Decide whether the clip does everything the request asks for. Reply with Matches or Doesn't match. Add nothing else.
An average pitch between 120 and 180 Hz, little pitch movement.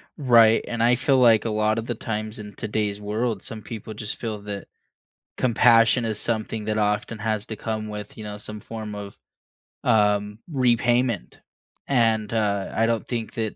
Doesn't match